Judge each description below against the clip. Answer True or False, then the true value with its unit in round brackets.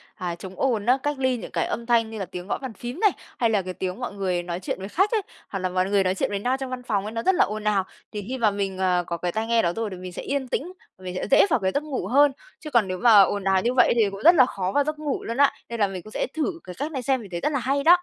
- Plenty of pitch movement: True (5.8 semitones)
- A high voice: True (220 Hz)